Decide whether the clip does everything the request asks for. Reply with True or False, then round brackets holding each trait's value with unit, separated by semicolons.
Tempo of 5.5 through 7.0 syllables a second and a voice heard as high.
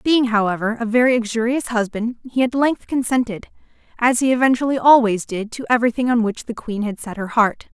True (5.7 syllables/s; 235 Hz)